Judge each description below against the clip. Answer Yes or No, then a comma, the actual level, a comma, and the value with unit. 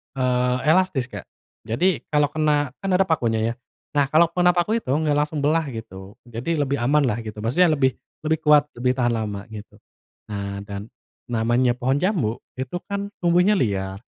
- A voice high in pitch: No, low, 135 Hz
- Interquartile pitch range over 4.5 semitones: Yes, wide, 5.6 semitones